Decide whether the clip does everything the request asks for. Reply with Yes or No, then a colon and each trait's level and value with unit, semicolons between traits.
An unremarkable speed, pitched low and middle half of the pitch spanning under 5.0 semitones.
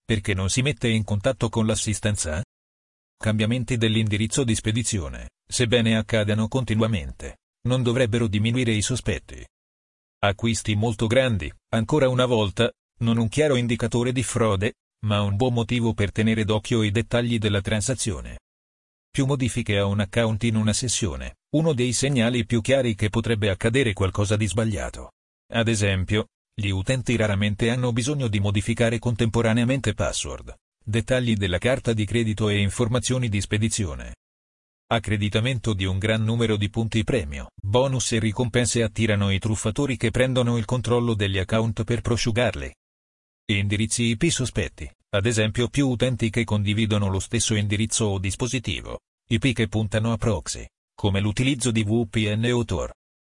Yes: average, 145 wpm; low, 110 Hz; average, 2.7 semitones